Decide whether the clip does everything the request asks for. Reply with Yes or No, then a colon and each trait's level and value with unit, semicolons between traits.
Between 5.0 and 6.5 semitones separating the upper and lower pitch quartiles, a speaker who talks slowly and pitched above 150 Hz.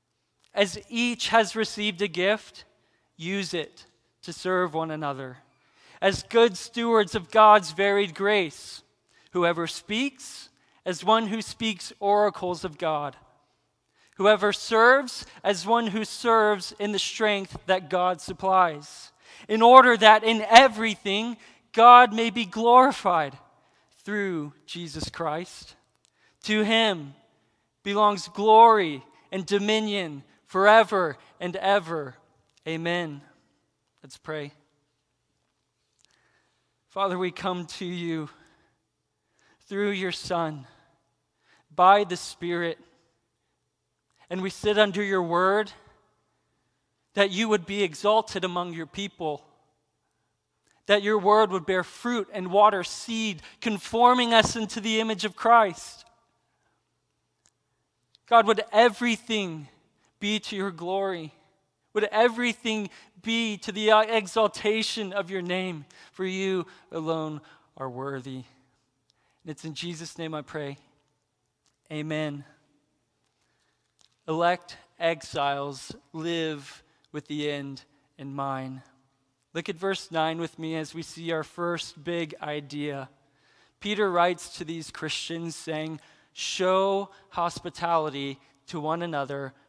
Yes: wide, 5.5 semitones; slow, 110 wpm; medium, 185 Hz